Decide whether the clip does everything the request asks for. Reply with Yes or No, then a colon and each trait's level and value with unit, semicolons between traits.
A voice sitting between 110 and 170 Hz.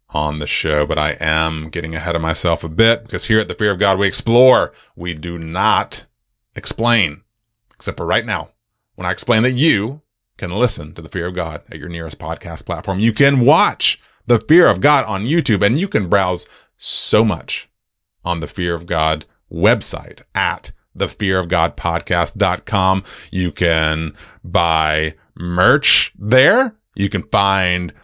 No: very low, 90 Hz